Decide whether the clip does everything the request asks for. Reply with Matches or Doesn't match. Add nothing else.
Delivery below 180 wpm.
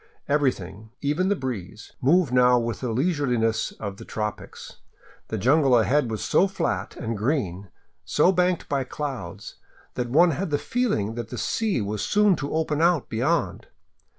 Matches